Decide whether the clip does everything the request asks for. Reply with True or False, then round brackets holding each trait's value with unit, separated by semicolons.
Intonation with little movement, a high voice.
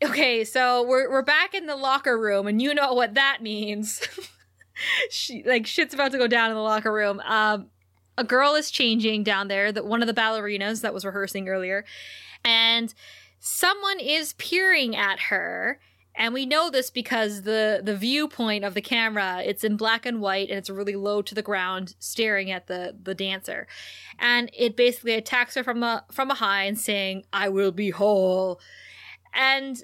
False (4.2 semitones; 225 Hz)